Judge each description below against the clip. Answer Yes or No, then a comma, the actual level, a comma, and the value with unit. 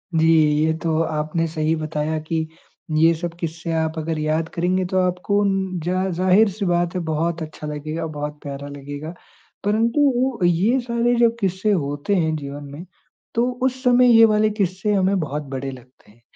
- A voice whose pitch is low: No, medium, 165 Hz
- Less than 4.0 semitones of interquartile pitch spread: No, average, 4.6 semitones